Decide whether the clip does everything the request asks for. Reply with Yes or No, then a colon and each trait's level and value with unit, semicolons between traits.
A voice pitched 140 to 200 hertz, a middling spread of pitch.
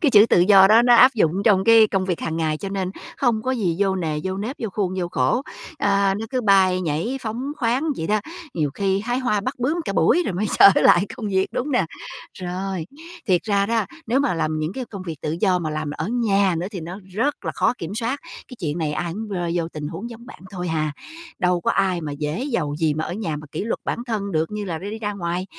Yes: high, 195 Hz; average, 4.8 semitones